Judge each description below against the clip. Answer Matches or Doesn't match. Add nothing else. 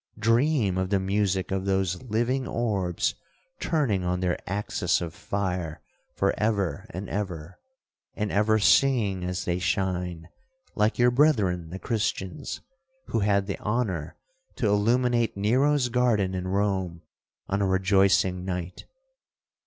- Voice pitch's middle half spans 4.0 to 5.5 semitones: Doesn't match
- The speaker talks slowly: Matches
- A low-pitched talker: Matches